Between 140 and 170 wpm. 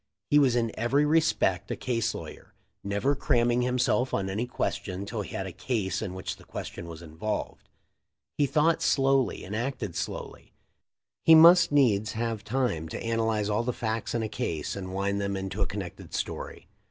No: average, 180 wpm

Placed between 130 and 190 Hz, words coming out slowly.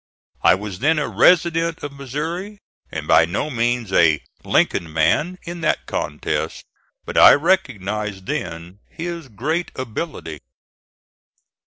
Yes: low, 135 Hz; slow, 125 wpm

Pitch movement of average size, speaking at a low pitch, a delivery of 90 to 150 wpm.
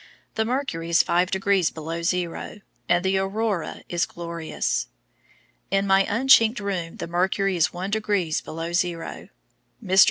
No: average, 3.0 semitones; medium, 185 Hz; average, 145 wpm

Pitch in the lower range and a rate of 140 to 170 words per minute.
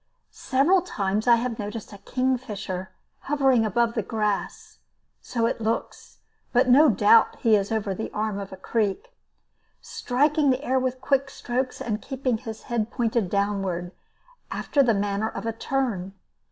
No: high, 230 Hz; average, 155 wpm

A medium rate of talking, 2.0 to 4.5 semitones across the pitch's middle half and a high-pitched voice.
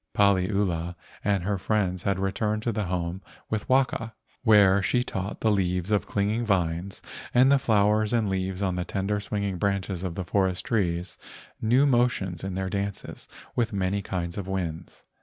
No: average, 175 wpm; narrow, 2.6 semitones; low, 100 Hz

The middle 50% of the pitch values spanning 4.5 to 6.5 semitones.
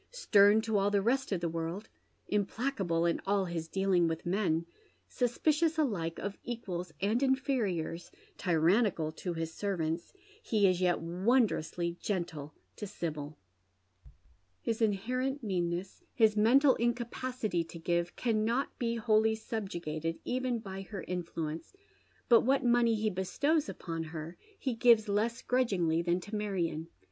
Yes: wide, 5.5 semitones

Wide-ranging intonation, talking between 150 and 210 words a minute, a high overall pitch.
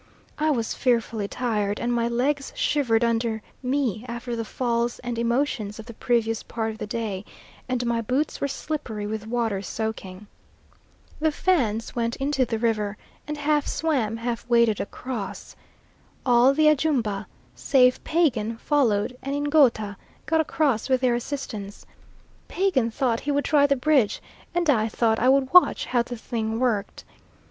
No: average, 3.8 semitones; average, 155 wpm; high, 240 Hz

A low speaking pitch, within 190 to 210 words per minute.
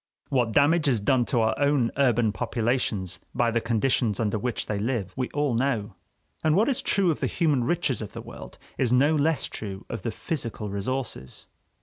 Yes: low, 120 Hz; average, 195 wpm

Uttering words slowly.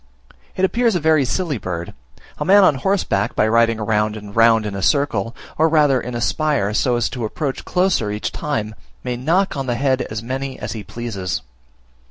No: average, 200 wpm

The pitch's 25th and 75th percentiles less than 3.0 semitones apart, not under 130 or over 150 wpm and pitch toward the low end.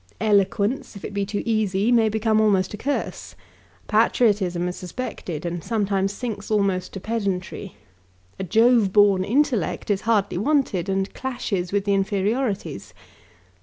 No: narrow, 2.6 semitones; average, 140 wpm; high, 205 Hz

